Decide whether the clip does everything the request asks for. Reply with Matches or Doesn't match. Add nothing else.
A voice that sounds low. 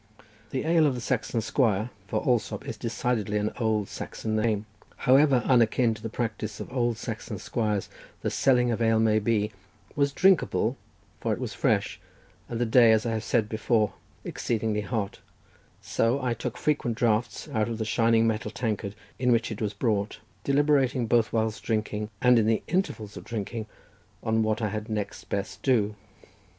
Matches